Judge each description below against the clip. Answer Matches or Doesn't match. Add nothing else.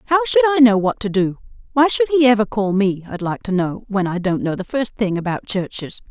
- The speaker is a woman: Matches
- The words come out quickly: Matches